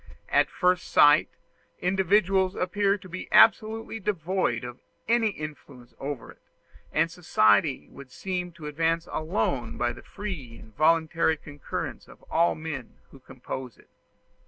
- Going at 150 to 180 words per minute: No, average, 140 wpm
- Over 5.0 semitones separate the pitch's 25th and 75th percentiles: Yes, wide, 5.5 semitones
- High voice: No, medium, 165 Hz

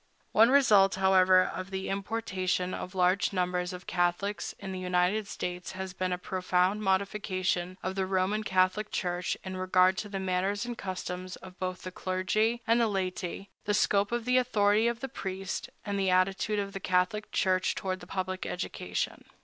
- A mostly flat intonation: Yes, narrow, 1.8 semitones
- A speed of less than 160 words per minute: No, average, 175 wpm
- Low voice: No, high, 190 Hz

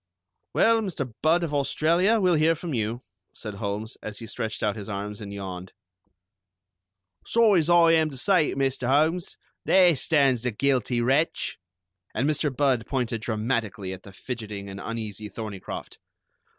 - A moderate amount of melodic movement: No, wide, 6.8 semitones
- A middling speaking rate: Yes, average, 160 wpm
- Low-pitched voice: Yes, low, 125 Hz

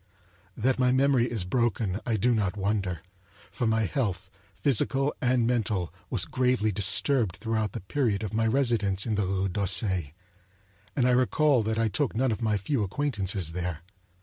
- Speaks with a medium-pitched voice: No, low, 110 Hz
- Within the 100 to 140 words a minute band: No, average, 170 wpm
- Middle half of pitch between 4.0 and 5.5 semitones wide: Yes, average, 4.3 semitones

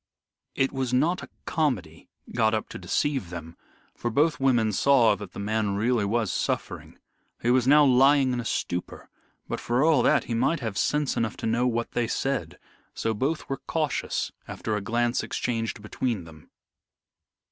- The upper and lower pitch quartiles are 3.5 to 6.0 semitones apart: Yes, average, 3.8 semitones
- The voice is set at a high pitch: No, low, 120 Hz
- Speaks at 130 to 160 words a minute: No, average, 175 wpm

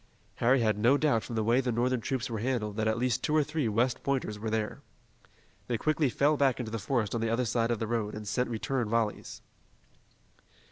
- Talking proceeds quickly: Yes, fast, 225 wpm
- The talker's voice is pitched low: Yes, low, 120 Hz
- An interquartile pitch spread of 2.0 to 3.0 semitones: Yes, average, 2.7 semitones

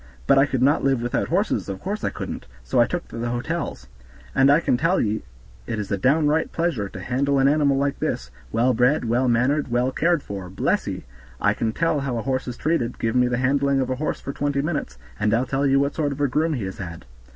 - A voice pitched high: No, low, 135 Hz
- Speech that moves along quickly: Yes, fast, 250 wpm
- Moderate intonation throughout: Yes, average, 3.4 semitones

